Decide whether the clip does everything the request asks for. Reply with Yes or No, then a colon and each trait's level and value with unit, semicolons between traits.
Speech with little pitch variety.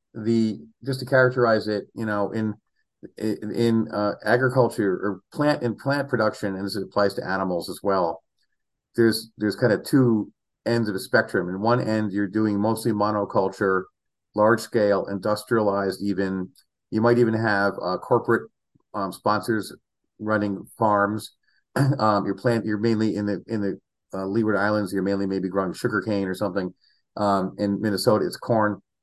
Yes: narrow, 2.3 semitones